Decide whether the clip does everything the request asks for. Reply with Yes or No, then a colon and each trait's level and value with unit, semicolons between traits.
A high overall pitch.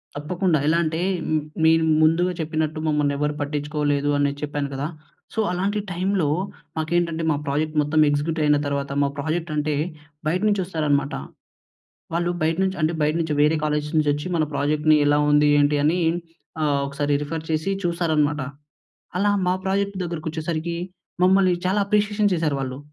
No: medium, 155 Hz